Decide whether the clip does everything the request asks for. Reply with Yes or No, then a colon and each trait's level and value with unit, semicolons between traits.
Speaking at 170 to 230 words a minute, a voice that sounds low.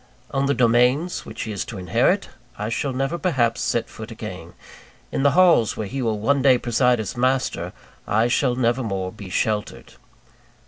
Yes: average, 180 wpm; low, 120 Hz